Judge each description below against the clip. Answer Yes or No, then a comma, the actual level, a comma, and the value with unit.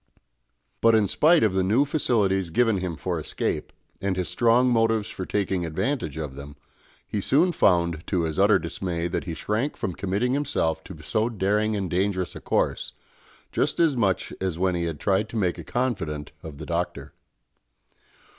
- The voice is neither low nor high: No, very low, 95 Hz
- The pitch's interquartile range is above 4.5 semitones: Yes, average, 4.9 semitones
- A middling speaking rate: Yes, average, 180 wpm